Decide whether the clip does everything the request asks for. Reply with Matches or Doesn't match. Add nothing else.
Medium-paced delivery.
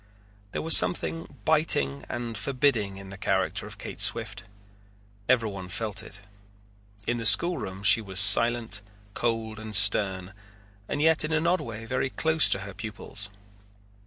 Matches